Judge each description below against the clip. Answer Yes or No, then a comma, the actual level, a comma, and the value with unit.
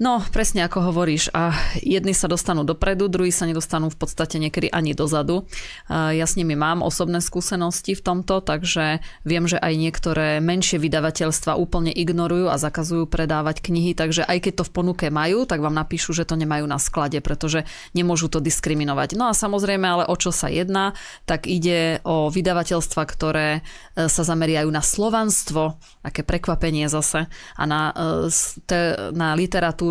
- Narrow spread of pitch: Yes, narrow, 2.2 semitones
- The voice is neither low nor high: Yes, medium, 165 Hz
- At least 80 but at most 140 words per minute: No, fast, 165 wpm